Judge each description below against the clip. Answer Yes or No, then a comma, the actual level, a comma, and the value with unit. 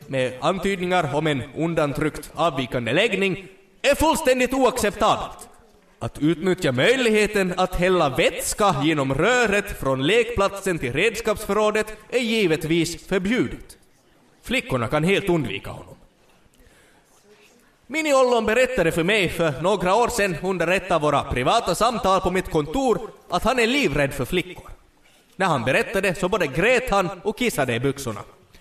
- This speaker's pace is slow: No, average, 135 wpm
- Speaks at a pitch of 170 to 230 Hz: Yes, medium, 185 Hz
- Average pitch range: No, wide, 5.7 semitones